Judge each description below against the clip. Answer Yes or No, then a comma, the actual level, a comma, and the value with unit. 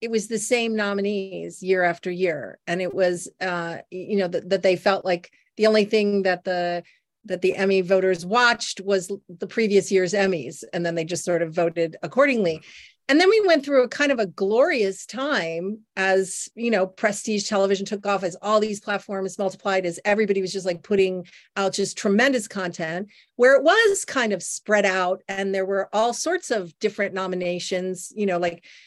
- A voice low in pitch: No, high, 195 Hz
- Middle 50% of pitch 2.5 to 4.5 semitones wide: Yes, average, 2.8 semitones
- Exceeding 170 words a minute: Yes, average, 195 wpm